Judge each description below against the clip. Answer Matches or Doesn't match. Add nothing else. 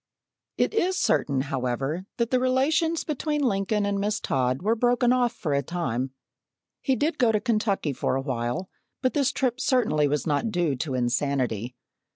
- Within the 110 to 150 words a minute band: Doesn't match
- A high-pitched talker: Matches